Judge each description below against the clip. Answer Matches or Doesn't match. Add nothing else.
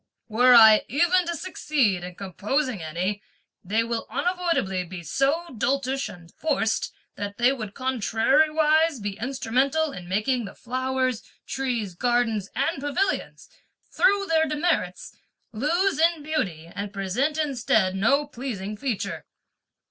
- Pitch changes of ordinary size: Doesn't match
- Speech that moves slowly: Matches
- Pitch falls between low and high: Doesn't match